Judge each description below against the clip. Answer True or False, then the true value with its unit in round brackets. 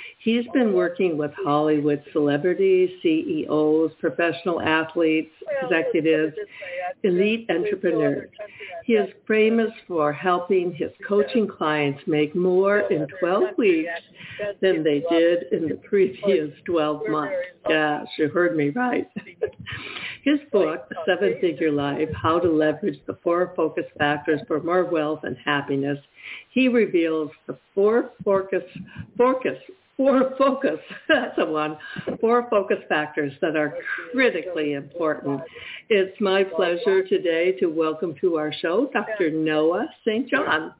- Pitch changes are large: True (6.1 semitones)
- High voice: False (180 Hz)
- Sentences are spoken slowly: True (125 wpm)